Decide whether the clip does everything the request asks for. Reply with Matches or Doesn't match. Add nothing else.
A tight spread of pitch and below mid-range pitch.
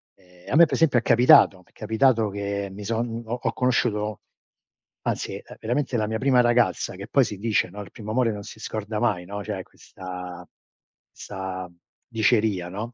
Doesn't match